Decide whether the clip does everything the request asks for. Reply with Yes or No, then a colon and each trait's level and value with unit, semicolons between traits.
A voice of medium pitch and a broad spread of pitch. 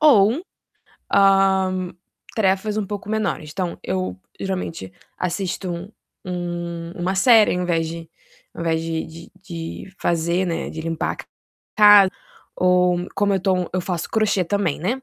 No: medium, 180 Hz; narrow, 2.6 semitones